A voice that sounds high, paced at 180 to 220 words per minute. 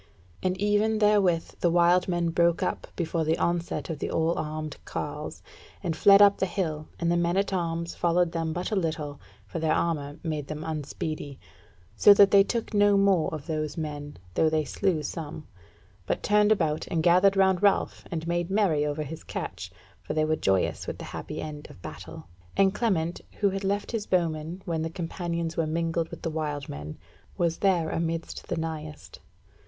No: medium, 170 Hz; average, 190 wpm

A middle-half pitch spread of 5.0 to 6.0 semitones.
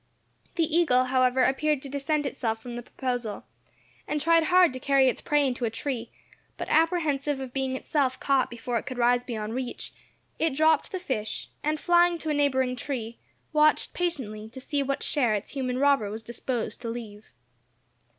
No: average, 3.6 semitones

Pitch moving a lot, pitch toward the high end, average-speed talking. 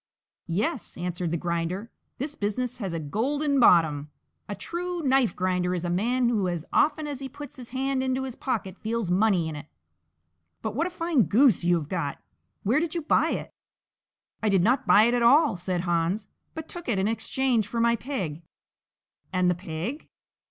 Yes: wide, 6.9 semitones; high, 220 Hz; average, 190 wpm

